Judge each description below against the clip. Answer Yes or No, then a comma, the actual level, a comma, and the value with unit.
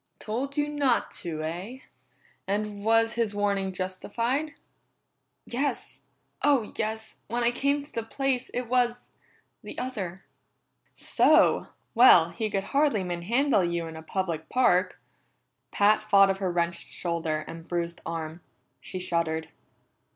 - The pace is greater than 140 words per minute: No, slow, 135 wpm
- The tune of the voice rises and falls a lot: Yes, wide, 6.0 semitones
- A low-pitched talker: No, high, 205 Hz